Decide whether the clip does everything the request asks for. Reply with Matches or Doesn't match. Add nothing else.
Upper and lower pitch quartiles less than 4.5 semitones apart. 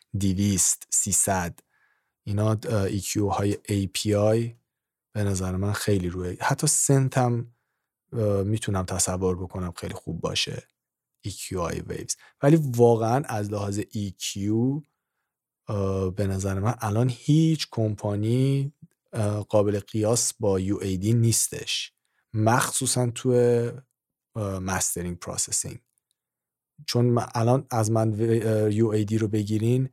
Matches